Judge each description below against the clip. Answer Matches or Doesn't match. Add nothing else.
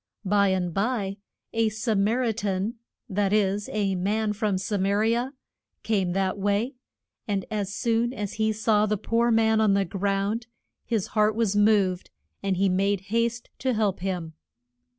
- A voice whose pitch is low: Doesn't match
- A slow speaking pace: Doesn't match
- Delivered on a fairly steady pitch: Matches